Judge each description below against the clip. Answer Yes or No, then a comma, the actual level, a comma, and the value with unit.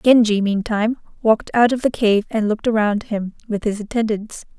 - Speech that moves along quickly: No, average, 185 wpm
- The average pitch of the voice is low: No, high, 220 Hz